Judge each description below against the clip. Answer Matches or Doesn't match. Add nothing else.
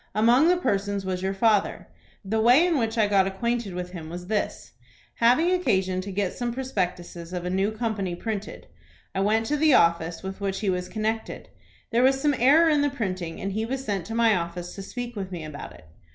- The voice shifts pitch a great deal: Doesn't match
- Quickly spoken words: Matches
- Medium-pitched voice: Doesn't match